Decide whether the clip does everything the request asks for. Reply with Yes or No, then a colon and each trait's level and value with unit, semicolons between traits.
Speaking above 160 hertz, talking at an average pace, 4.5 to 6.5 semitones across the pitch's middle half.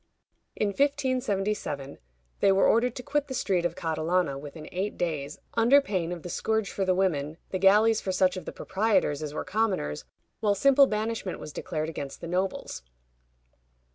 Yes: high, 190 Hz; average, 170 wpm; average, 5.1 semitones